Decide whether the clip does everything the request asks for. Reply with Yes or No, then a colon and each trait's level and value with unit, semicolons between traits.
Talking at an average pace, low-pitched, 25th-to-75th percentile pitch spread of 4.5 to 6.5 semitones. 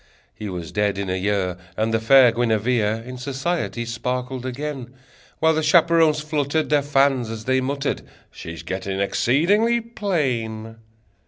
Yes: average, 145 wpm; low, 125 Hz; average, 5.3 semitones